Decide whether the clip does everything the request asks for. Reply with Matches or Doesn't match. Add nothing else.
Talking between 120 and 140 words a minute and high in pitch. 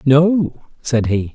Doesn't match